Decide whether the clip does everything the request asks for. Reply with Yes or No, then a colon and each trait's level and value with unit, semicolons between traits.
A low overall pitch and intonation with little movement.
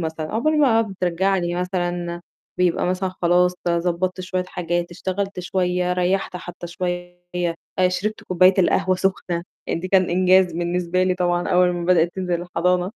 No: medium, 180 Hz; narrow, 1.0 semitones